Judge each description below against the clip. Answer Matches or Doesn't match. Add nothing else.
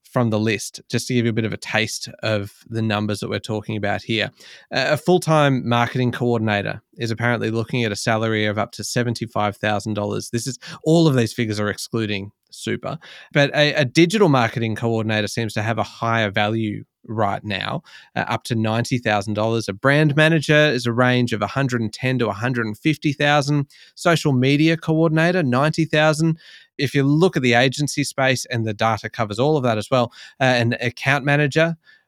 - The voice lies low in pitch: Matches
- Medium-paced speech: Matches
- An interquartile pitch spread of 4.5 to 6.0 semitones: Matches